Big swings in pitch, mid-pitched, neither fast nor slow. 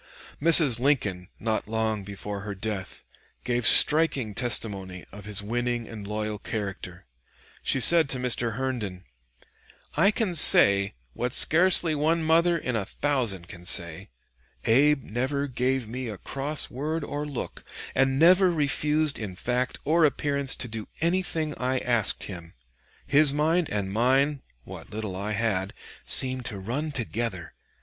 No: wide, 5.9 semitones; low, 125 Hz; average, 145 wpm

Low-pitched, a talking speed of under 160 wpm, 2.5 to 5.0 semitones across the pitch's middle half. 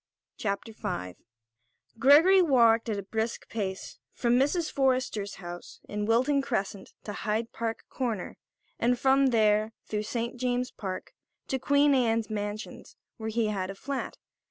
No: high, 225 Hz; average, 145 wpm; average, 3.7 semitones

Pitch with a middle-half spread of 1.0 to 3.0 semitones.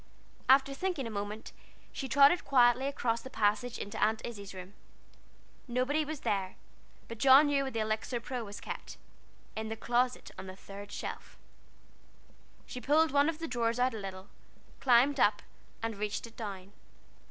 No: average, 4.5 semitones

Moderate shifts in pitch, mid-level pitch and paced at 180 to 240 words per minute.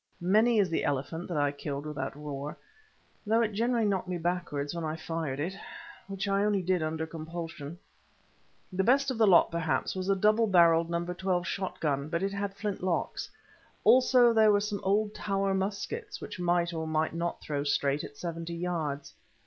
Yes: average, 4.0 semitones; medium, 175 Hz; average, 190 wpm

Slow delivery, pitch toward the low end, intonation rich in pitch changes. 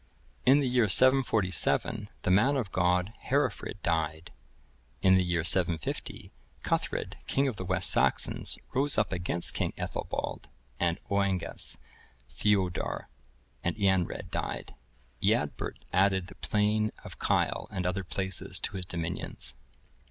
No: slow, 130 wpm; very low, 95 Hz; average, 3.3 semitones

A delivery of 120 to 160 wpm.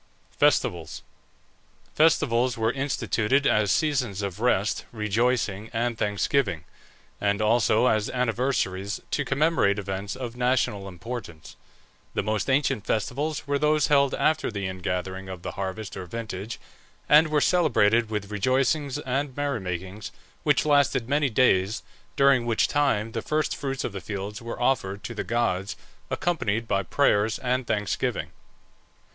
Yes: average, 140 wpm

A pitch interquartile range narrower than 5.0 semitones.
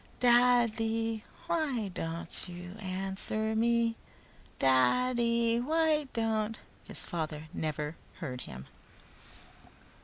No: wide, 5.5 semitones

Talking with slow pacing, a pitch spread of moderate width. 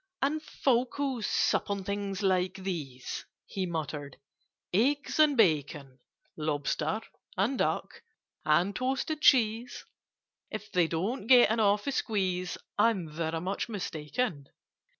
No: slow, 110 wpm; wide, 6.6 semitones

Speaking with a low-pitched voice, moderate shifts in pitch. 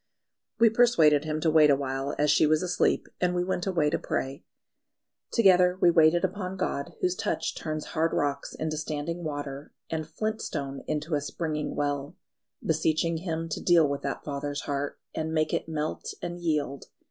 No: medium, 155 Hz; average, 3.1 semitones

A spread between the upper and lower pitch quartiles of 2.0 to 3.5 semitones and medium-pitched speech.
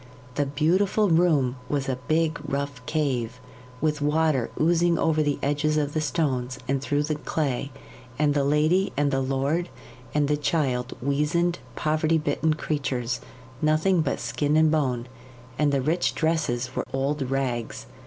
Yes: narrow, 2.6 semitones; medium, 145 Hz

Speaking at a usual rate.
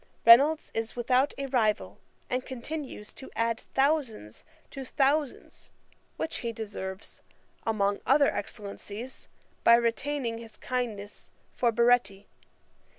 No: slow, 110 wpm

